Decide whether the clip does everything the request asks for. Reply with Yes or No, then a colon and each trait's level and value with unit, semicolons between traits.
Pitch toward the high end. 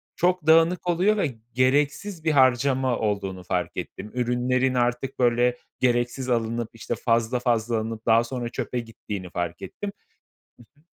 No: low, 125 Hz